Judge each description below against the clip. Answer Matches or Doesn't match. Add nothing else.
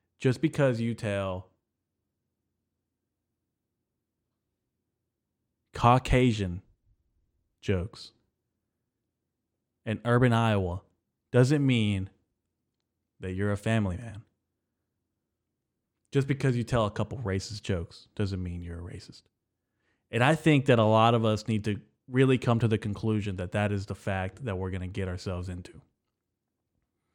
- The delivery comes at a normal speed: Doesn't match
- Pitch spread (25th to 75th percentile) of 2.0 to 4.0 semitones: Matches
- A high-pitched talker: Doesn't match